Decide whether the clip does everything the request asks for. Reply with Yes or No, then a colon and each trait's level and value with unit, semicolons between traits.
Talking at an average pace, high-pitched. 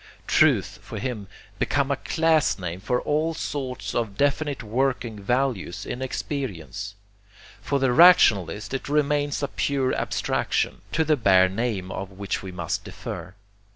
No: average, 145 wpm; low, 125 Hz